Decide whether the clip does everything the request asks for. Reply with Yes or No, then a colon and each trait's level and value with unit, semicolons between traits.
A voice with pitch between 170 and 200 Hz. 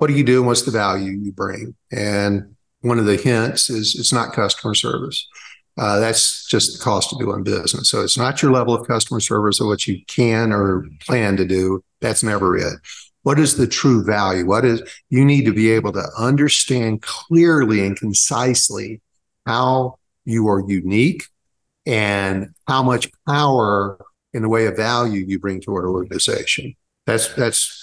No: low, 110 Hz